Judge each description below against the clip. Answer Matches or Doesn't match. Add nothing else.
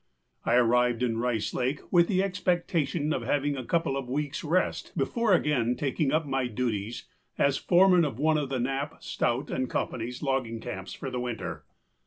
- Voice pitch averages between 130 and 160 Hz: Matches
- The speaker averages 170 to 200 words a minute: Matches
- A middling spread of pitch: Matches